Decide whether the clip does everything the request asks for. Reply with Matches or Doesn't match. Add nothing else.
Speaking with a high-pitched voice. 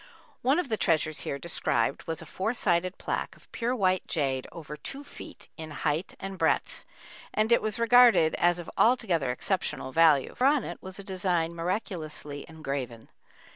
Doesn't match